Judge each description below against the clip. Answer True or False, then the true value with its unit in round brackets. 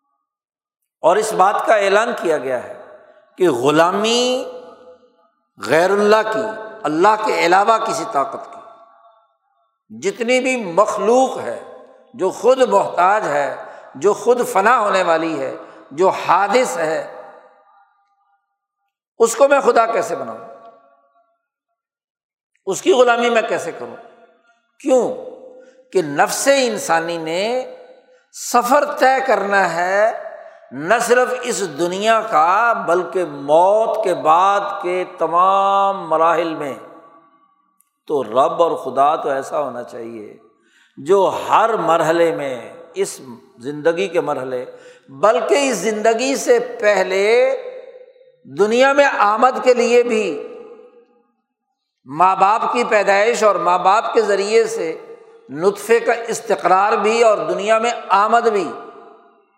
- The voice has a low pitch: False (230 Hz)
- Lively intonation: True (6.1 semitones)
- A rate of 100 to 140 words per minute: True (115 wpm)